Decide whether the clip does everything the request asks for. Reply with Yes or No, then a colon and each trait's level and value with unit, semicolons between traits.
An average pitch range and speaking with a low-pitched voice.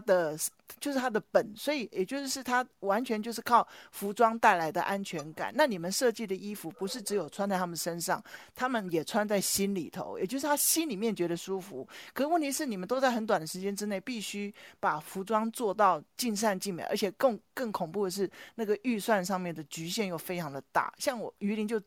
No: average, 4.1 semitones; high, 205 Hz